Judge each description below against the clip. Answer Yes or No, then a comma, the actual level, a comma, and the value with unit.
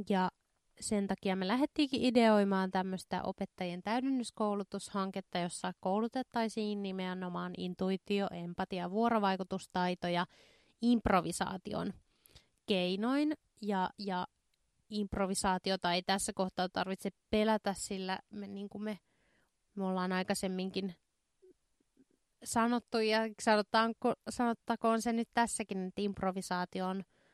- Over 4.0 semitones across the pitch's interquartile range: No, average, 2.8 semitones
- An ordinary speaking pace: No, slow, 90 wpm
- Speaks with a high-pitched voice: Yes, high, 195 Hz